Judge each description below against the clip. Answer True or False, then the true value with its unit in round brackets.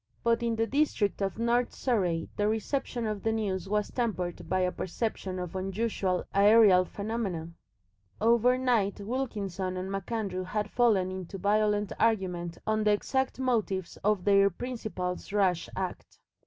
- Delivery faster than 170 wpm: False (140 wpm)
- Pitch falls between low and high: False (205 Hz)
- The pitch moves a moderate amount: True (3.4 semitones)